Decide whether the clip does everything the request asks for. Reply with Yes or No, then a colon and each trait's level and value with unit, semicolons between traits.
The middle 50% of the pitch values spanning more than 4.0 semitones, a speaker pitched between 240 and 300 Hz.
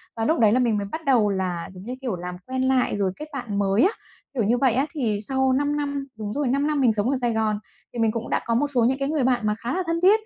Yes: average, 4.6 semitones; high, 245 Hz